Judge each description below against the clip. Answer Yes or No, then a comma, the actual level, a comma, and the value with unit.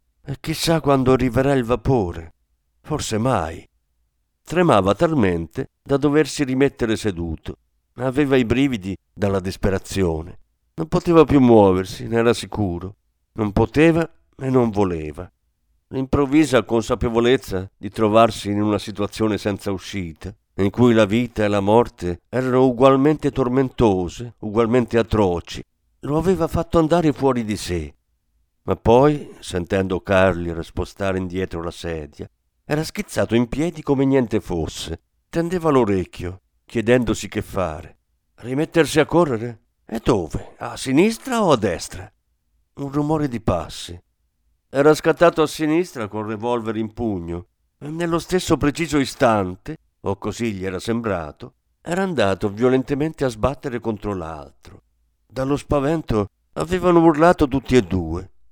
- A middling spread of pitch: No, wide, 7.3 semitones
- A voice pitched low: Yes, low, 110 Hz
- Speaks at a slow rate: No, average, 130 wpm